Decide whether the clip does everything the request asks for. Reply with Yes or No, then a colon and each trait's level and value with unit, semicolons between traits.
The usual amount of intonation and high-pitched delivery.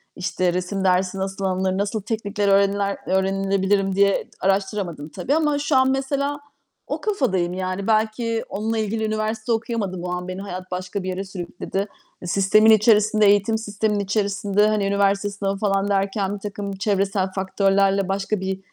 No: narrow, 2.1 semitones; high, 200 Hz